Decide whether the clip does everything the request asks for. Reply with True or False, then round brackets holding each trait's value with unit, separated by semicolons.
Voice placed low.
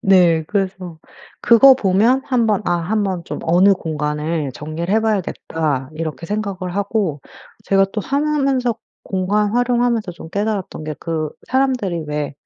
False (195 Hz)